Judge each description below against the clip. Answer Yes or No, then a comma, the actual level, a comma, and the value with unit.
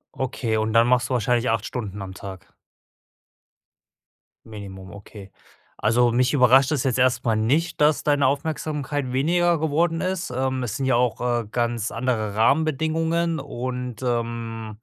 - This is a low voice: Yes, low, 125 Hz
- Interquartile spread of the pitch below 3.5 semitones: No, average, 4.2 semitones